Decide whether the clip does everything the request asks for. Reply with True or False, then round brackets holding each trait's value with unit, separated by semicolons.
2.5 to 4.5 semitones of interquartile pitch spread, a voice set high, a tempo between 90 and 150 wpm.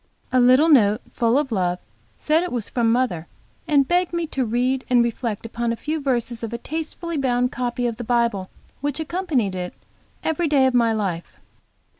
False (4.1 semitones; 245 Hz; 190 wpm)